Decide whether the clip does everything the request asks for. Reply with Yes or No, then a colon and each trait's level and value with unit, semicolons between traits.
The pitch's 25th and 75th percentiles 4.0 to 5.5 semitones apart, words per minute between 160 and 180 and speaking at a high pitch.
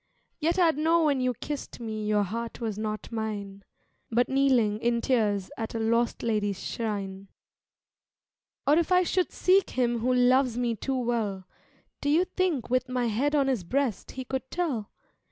Yes: average, 4.3 semitones; average, 170 wpm; high, 240 Hz